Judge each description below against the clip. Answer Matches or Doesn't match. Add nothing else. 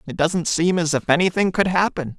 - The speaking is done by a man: Matches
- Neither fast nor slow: Doesn't match